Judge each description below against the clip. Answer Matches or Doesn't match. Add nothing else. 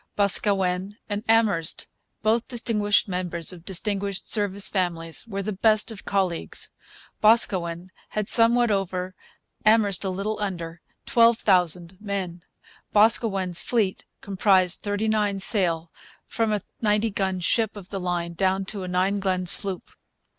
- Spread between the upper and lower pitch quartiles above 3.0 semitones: Doesn't match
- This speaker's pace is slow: Matches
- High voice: Matches